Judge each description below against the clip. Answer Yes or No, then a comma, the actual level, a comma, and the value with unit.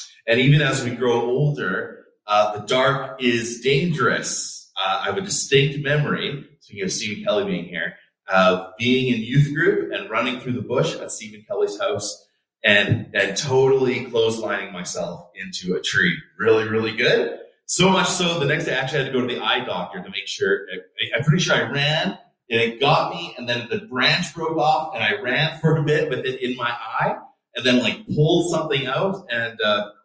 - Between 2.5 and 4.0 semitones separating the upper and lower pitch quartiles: No, average, 5.1 semitones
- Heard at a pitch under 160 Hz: Yes, low, 135 Hz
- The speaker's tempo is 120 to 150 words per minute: No, fast, 205 wpm